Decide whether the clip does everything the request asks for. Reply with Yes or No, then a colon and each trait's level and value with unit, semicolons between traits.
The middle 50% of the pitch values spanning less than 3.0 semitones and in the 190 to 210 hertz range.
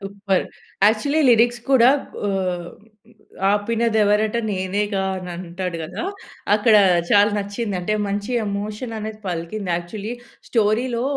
Yes: narrow, 2.6 semitones; high, 205 Hz